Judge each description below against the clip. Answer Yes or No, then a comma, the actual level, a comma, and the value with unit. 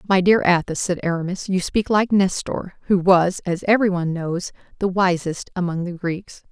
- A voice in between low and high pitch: Yes, medium, 180 Hz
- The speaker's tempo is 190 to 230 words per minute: No, average, 175 wpm